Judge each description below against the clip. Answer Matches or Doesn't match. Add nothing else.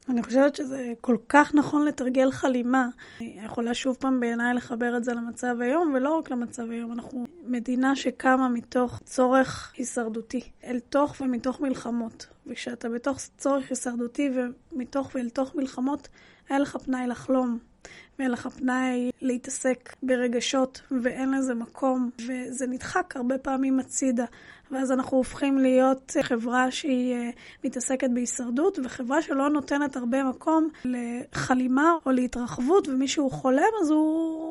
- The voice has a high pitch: Matches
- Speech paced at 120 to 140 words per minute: Matches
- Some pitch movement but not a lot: Doesn't match